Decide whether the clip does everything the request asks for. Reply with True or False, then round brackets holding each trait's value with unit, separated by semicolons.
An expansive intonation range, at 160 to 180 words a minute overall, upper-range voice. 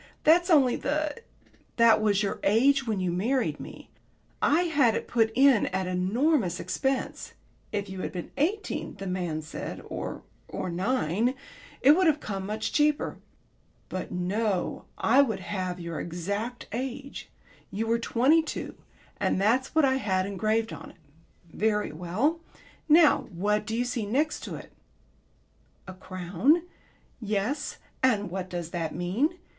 False (6.5 semitones; 150 wpm; 220 Hz)